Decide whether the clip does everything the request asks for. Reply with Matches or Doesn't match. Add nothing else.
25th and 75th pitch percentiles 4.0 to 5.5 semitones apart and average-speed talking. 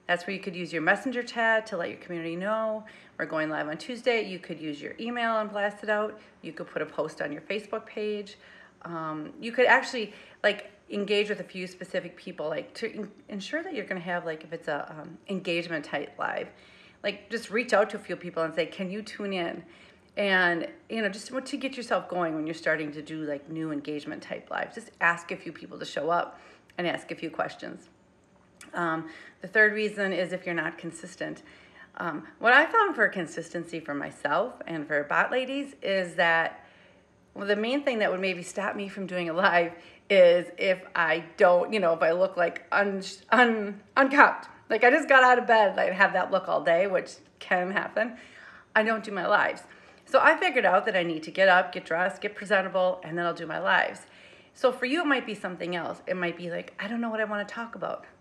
Doesn't match